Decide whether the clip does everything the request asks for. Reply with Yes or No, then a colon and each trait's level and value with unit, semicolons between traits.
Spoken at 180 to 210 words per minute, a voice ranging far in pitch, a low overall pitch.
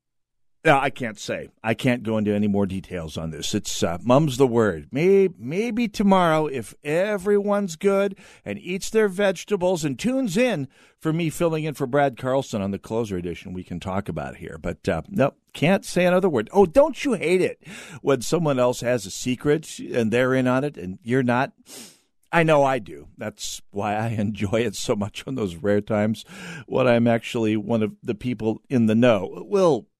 Yes: average, 200 wpm; wide, 8.9 semitones; low, 130 Hz